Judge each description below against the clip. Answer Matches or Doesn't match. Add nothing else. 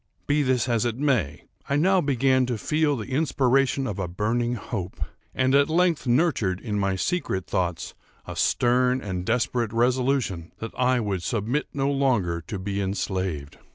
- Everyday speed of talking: Matches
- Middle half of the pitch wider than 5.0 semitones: Matches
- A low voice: Matches